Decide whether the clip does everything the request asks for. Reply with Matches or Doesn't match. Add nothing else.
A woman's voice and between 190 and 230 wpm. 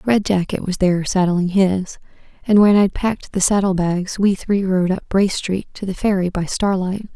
Matches